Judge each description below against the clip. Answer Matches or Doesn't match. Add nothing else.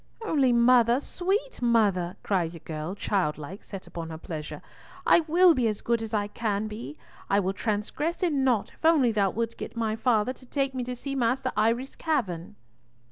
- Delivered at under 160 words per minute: Doesn't match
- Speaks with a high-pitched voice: Matches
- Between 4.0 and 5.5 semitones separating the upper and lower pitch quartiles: Matches